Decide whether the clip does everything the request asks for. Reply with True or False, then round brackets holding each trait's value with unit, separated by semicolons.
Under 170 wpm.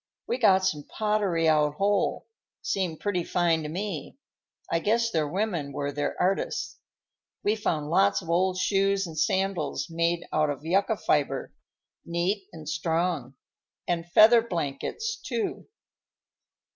True (135 wpm)